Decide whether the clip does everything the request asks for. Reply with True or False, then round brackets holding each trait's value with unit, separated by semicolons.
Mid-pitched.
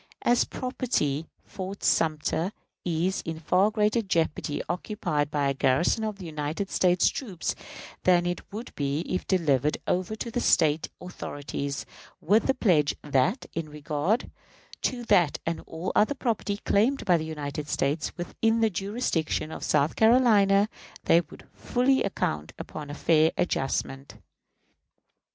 True (175 Hz)